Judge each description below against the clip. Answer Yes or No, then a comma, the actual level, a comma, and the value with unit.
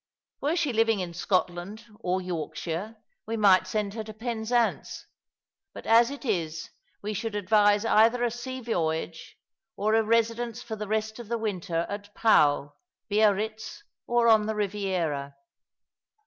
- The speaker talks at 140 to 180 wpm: Yes, average, 150 wpm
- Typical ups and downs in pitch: Yes, average, 3.6 semitones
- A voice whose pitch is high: Yes, high, 215 Hz